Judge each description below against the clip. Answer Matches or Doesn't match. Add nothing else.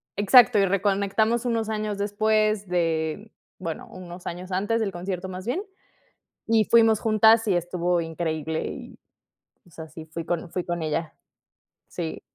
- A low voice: Doesn't match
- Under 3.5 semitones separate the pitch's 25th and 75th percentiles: Doesn't match